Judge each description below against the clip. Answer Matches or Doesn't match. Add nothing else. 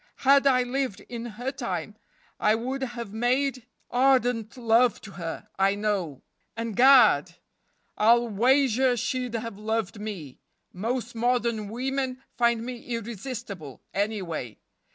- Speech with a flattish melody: Doesn't match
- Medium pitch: Doesn't match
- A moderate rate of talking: Doesn't match